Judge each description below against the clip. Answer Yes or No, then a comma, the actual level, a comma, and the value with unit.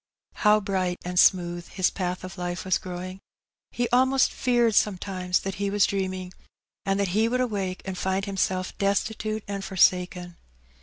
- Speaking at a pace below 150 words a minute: No, average, 160 wpm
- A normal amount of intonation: No, narrow, 2.1 semitones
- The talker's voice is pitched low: No, high, 190 Hz